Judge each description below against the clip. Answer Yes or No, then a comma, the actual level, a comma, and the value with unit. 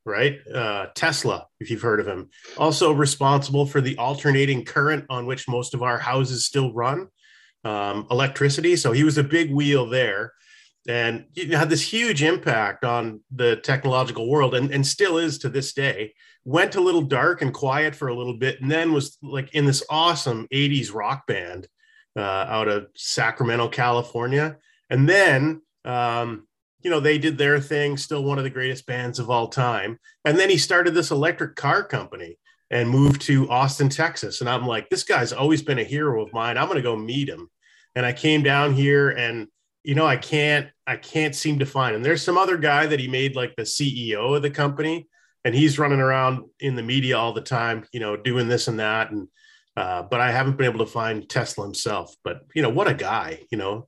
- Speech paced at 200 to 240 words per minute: Yes, fast, 205 wpm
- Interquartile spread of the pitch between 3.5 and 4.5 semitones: Yes, average, 3.8 semitones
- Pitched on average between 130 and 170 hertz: Yes, low, 135 Hz